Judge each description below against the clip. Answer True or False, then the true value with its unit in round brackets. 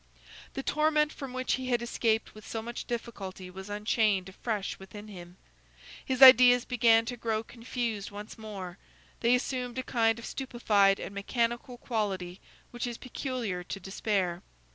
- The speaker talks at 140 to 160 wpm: True (155 wpm)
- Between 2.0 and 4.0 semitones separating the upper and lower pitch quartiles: True (3.7 semitones)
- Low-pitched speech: False (225 Hz)